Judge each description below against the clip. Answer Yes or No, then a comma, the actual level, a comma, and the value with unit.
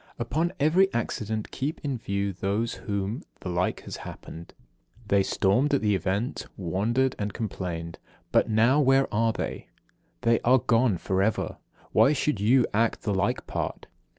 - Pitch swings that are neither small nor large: Yes, average, 4.7 semitones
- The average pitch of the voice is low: Yes, low, 110 Hz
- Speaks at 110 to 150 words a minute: No, average, 165 wpm